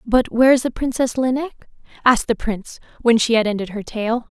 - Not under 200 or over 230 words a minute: Yes, fast, 205 wpm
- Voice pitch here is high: Yes, high, 235 Hz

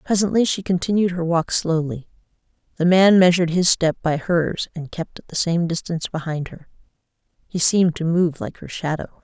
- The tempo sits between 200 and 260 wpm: No, average, 180 wpm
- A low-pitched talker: No, medium, 170 Hz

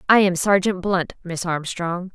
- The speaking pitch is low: No, medium, 180 Hz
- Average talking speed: Yes, average, 170 wpm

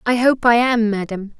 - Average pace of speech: No, fast, 215 wpm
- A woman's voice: Yes, female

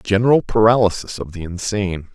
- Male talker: Yes, male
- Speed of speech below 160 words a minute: Yes, average, 140 wpm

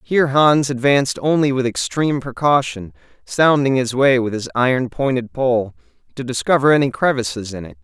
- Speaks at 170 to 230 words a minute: No, average, 160 wpm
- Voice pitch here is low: Yes, low, 130 Hz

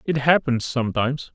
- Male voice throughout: Yes, male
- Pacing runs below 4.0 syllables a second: No, 5.6 syllables/s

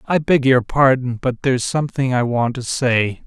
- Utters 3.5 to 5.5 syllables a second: Yes, 4.9 syllables/s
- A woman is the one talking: No, male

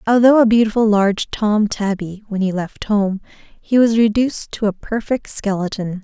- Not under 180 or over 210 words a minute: No, average, 170 wpm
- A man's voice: No, female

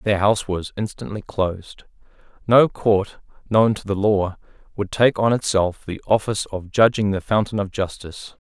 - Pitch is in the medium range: No, low, 100 Hz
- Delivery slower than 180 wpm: Yes, average, 165 wpm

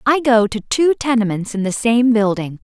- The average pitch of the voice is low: No, high, 230 Hz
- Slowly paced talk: No, average, 200 wpm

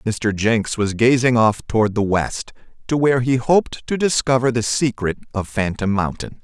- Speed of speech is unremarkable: Yes, average, 170 wpm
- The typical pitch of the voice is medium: No, low, 115 Hz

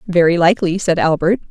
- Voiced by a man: No, female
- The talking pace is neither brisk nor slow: Yes, average, 160 wpm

